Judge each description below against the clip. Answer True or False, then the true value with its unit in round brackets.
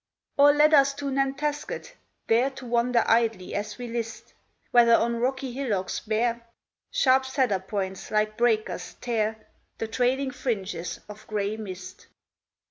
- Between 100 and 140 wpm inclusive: True (135 wpm)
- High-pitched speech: True (235 Hz)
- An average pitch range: True (3.8 semitones)